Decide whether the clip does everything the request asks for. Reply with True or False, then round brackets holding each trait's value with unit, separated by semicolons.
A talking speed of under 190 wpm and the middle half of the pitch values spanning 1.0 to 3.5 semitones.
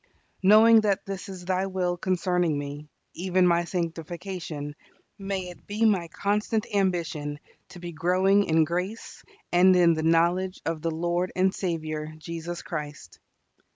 True (145 wpm; 2.5 semitones)